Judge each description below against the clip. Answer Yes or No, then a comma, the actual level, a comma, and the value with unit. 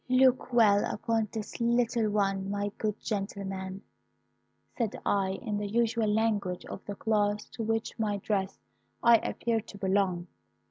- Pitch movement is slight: Yes, narrow, 2.3 semitones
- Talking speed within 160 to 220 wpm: No, average, 150 wpm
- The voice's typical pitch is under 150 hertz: No, high, 210 Hz